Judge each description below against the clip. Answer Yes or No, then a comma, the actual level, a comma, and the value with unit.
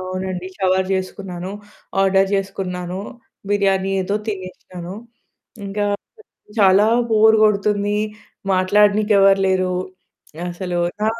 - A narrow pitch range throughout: Yes, narrow, 1.6 semitones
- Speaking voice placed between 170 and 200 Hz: Yes, high, 190 Hz